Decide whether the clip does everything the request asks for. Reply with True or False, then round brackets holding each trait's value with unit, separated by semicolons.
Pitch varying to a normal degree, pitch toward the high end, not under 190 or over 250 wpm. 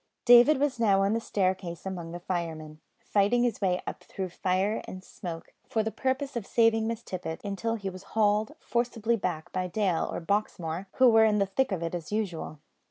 True (4.0 semitones; 200 Hz; 200 wpm)